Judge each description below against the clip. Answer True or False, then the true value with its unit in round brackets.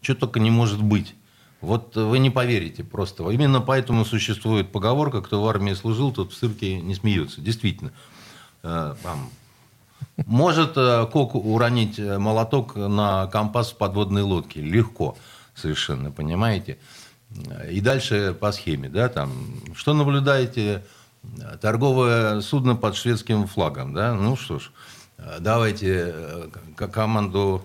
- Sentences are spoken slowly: False (120 wpm)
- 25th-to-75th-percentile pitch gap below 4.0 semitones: True (3.6 semitones)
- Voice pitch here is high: False (110 Hz)